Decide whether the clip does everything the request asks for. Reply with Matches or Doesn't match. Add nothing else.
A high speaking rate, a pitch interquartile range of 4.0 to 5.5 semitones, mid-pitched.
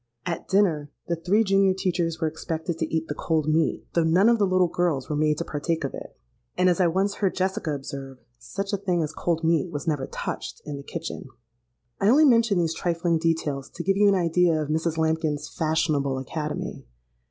Doesn't match